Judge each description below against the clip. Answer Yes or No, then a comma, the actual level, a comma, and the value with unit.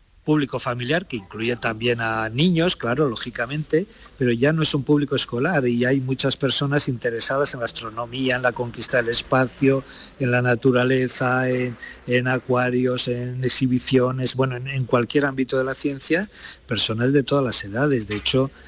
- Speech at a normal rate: Yes, average, 165 wpm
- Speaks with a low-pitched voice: Yes, low, 130 Hz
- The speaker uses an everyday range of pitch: No, narrow, 2.2 semitones